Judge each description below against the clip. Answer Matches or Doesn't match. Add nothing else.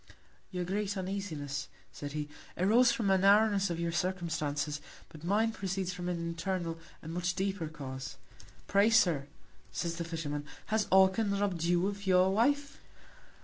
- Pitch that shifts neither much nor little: Matches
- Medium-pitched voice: Matches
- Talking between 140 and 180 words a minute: Matches